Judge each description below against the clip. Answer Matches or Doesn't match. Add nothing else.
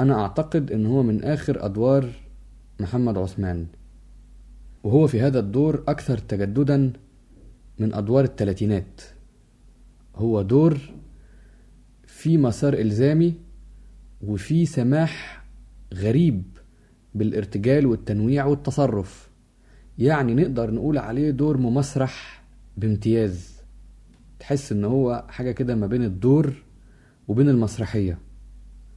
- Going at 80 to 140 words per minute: Matches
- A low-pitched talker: Matches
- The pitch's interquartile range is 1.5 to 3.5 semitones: Doesn't match